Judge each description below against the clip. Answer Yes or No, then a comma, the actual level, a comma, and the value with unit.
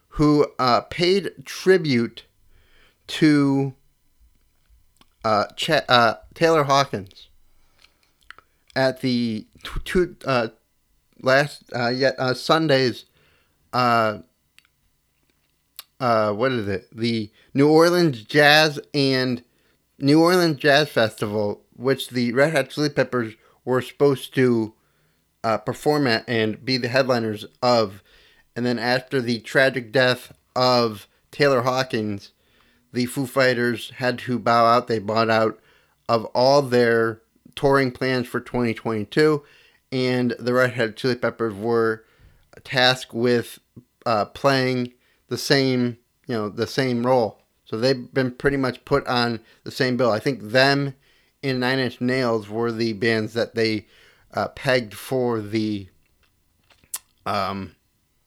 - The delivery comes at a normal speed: No, slow, 125 wpm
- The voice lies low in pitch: Yes, low, 125 Hz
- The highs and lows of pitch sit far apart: No, average, 3.1 semitones